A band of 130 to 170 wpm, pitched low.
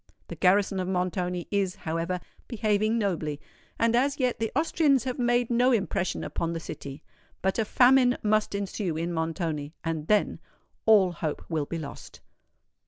No: average, 155 wpm; high, 195 Hz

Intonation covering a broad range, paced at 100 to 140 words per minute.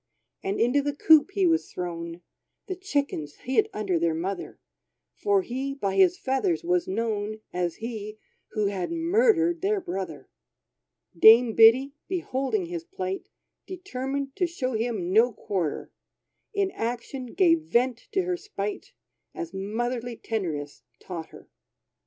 Yes: wide, 9.0 semitones; slow, 135 wpm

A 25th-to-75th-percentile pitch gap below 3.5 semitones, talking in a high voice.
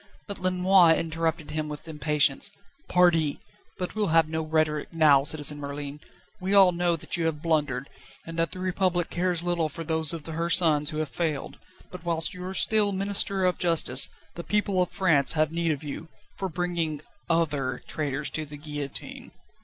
No: average, 3.0 semitones; medium, 165 Hz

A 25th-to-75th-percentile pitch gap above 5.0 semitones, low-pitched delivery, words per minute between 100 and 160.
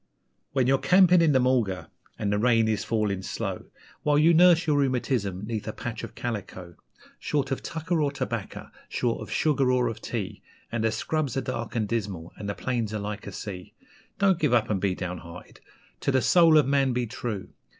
No: wide, 5.5 semitones; low, 120 Hz; fast, 205 wpm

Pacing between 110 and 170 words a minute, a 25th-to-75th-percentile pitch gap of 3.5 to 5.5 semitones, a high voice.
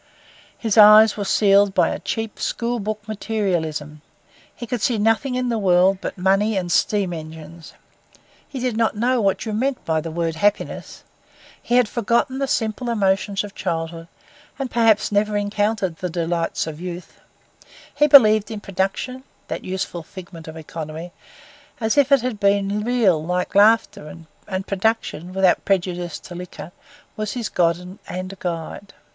Yes: average, 160 wpm; average, 4.0 semitones; high, 200 Hz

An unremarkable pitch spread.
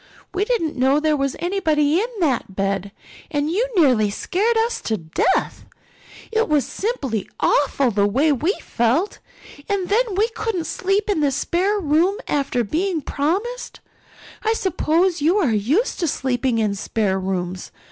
No: wide, 8.2 semitones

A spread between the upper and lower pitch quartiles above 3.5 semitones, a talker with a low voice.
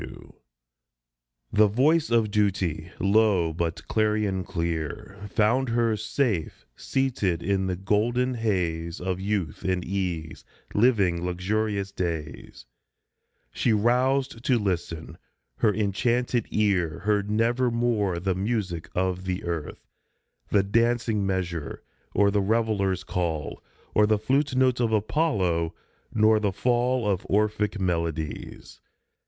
Yes: average, 4.0 semitones; low, 100 Hz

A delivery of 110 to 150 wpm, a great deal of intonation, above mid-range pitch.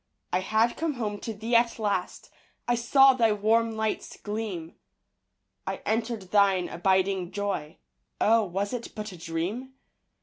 No: average, 145 wpm; average, 3.3 semitones; high, 210 Hz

